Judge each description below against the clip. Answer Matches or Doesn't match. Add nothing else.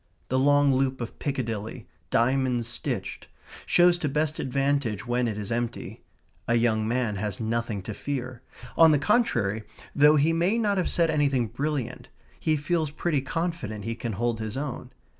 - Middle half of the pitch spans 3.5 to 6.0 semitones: Matches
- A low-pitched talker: Matches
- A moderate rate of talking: Matches